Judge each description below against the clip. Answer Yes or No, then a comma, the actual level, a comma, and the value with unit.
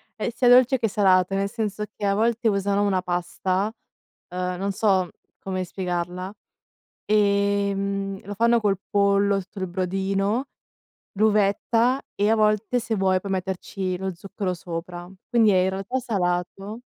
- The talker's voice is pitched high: Yes, high, 200 Hz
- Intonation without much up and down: Yes, narrow, 2.3 semitones